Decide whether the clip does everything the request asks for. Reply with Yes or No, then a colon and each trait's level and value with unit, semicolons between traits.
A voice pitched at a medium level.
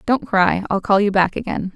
No: high, 205 Hz